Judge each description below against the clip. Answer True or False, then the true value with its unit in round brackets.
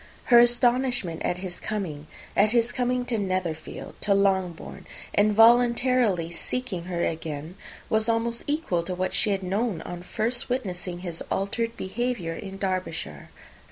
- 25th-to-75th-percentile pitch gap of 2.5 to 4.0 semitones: False (5.1 semitones)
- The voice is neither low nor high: False (200 Hz)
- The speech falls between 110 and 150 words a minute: True (145 wpm)